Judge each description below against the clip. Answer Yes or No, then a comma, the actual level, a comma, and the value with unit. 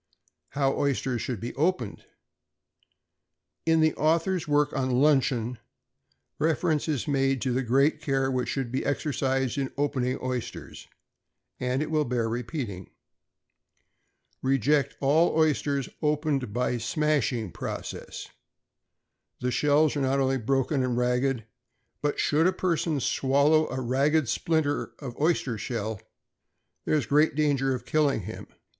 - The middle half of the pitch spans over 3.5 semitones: No, average, 3.2 semitones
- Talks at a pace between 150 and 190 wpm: No, slow, 135 wpm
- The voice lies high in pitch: No, low, 135 Hz